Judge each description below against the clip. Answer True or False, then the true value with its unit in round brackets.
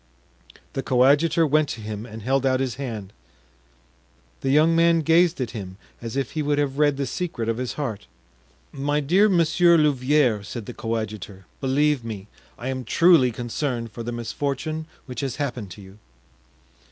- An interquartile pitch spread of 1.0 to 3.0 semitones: False (4.6 semitones)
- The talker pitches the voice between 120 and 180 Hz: True (135 Hz)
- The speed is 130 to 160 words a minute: False (170 wpm)